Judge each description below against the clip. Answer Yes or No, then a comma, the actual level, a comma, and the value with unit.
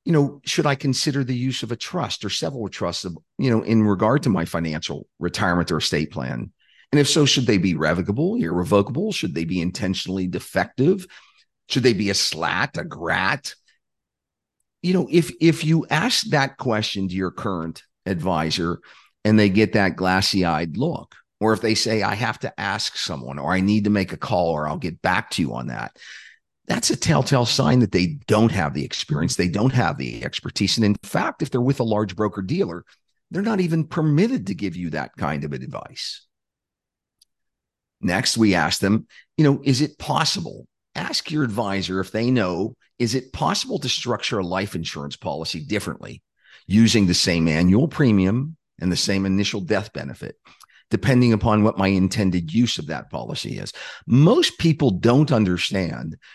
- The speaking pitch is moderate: No, low, 105 Hz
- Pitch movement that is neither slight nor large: No, wide, 6.7 semitones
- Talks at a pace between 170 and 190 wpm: Yes, average, 185 wpm